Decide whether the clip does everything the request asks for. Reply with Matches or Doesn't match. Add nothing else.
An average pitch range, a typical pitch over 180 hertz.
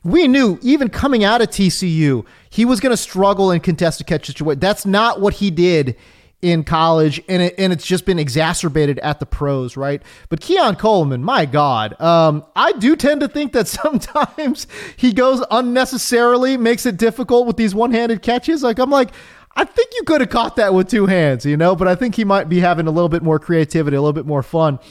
Doesn't match